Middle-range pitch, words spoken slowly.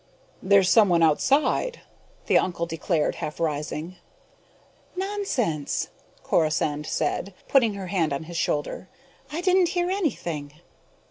Yes: medium, 180 Hz; slow, 115 wpm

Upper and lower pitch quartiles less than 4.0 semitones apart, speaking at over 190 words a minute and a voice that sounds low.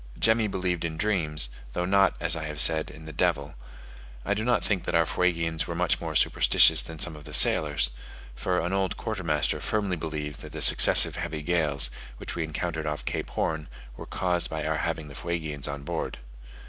Yes: average, 2.9 semitones; average, 200 wpm; very low, 80 Hz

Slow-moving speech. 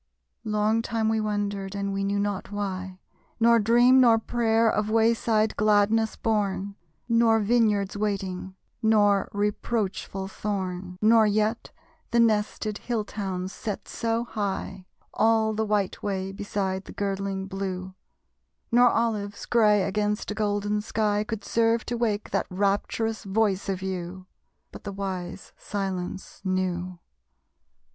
Yes: slow, 130 wpm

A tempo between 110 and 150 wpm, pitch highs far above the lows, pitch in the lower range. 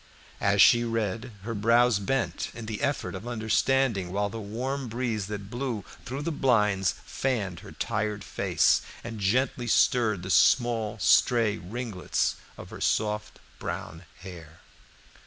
No: average, 140 wpm; average, 3.2 semitones; low, 110 Hz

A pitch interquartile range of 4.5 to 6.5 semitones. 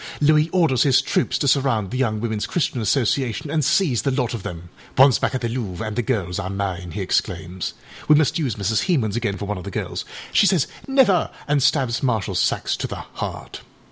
Yes: wide, 5.6 semitones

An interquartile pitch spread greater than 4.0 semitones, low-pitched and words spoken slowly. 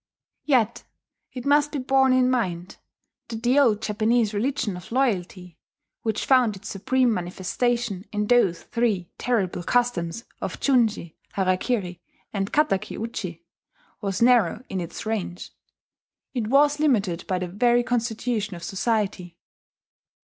No: average, 4.8 semitones; high, 220 Hz; slow, 130 wpm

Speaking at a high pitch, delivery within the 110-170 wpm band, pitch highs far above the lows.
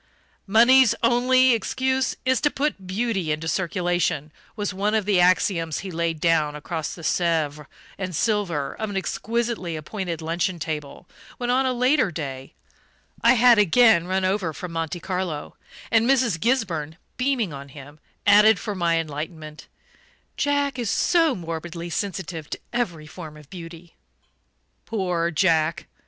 No: medium, 180 Hz; average, 145 wpm; wide, 5.9 semitones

